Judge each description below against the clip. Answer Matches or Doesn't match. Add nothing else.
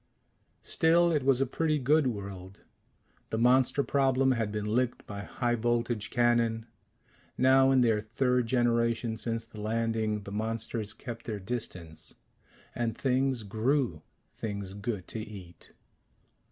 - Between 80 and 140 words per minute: Matches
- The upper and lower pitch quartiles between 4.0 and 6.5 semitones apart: Doesn't match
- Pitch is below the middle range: Matches